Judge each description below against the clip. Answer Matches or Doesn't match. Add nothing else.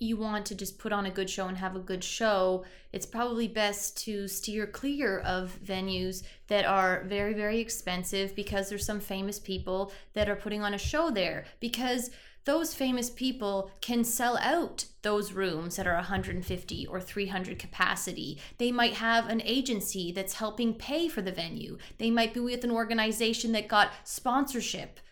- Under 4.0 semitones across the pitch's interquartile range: Matches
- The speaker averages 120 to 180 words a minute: Matches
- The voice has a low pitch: Doesn't match